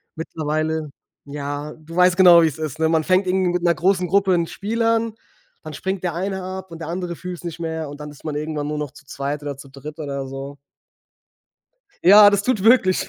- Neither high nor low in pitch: Yes, medium, 165 Hz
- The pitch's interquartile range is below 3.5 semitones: No, average, 3.9 semitones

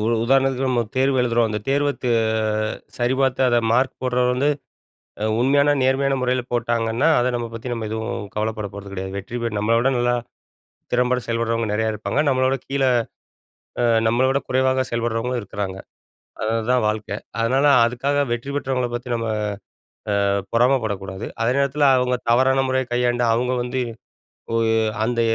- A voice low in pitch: Yes, low, 125 Hz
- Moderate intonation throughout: No, narrow, 2.3 semitones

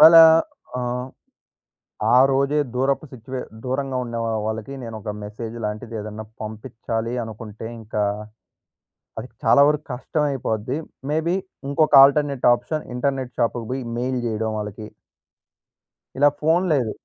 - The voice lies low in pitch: Yes, low, 125 Hz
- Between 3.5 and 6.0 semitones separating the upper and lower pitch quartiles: Yes, average, 3.9 semitones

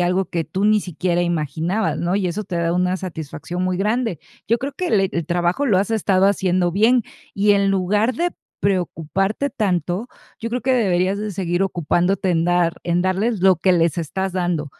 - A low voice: No, medium, 185 Hz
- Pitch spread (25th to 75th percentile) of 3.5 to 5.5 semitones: No, average, 2.9 semitones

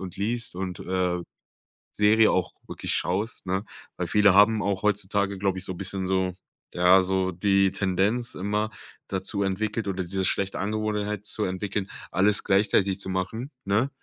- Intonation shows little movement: Yes, narrow, 1.9 semitones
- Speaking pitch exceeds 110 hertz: No, low, 100 Hz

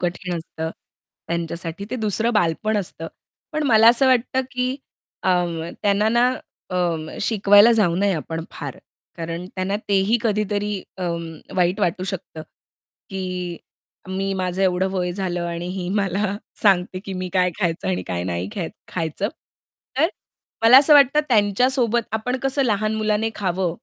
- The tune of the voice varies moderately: Yes, average, 3.7 semitones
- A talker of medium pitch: No, high, 195 Hz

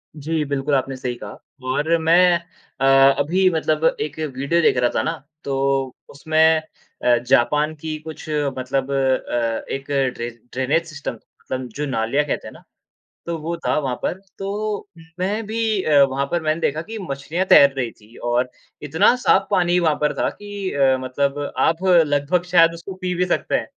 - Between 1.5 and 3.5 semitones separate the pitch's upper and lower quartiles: No, average, 4.1 semitones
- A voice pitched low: No, medium, 150 Hz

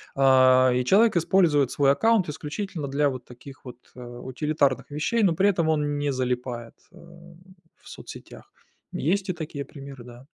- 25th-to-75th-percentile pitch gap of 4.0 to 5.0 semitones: Yes, average, 4.7 semitones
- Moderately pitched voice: Yes, medium, 145 Hz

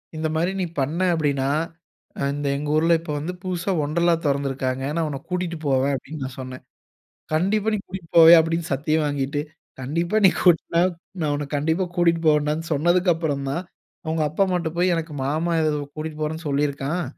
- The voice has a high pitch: No, medium, 155 Hz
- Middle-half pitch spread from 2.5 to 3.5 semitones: Yes, average, 3.0 semitones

